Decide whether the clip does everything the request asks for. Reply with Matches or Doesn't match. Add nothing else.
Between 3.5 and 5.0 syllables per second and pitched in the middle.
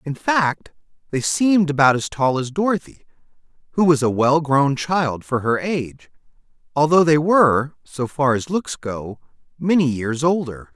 Matches